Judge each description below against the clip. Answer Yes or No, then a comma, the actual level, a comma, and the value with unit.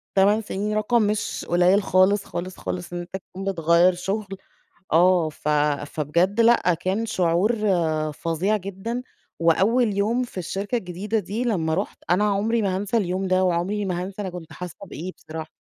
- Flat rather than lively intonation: No, average, 3.0 semitones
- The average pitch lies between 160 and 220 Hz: Yes, high, 190 Hz